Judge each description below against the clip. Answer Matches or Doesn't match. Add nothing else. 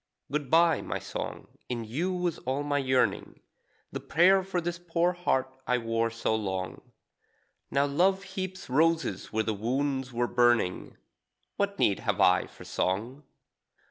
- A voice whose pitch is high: Doesn't match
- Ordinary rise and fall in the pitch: Doesn't match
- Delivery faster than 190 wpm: Doesn't match